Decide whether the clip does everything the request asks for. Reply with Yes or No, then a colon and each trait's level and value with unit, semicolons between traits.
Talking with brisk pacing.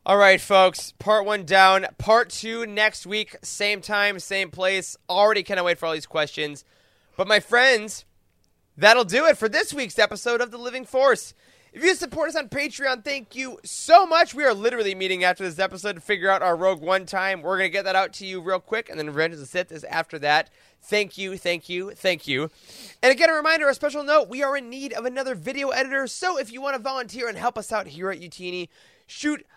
Yes: fast, 230 wpm